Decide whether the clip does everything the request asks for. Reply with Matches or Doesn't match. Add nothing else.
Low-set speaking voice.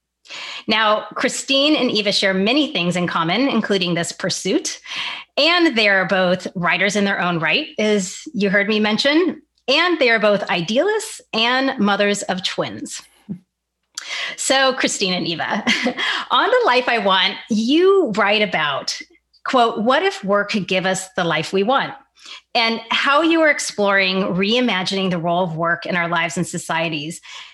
Doesn't match